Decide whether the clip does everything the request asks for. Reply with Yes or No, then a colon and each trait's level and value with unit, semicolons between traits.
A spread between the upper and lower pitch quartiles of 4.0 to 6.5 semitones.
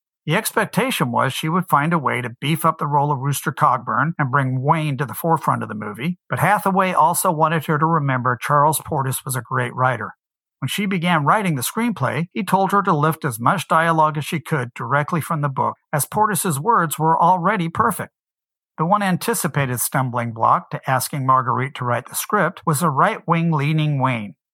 Yes: average, 4.4 semitones